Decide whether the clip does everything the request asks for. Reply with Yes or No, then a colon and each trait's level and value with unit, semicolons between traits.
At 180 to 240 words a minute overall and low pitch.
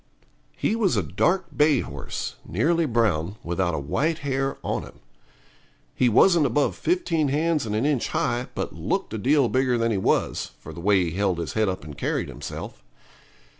Yes: average, 185 wpm; low, 120 Hz